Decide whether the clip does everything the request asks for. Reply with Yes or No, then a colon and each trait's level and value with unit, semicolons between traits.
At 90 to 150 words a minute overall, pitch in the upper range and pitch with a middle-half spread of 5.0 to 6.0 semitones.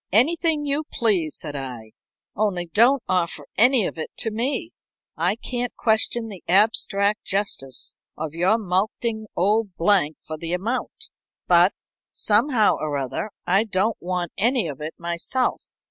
Yes: average, 145 wpm; high, 200 Hz; wide, 5.4 semitones